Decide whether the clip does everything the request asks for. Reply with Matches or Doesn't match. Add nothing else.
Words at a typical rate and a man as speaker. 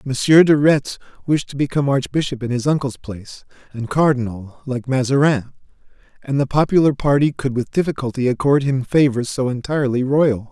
Matches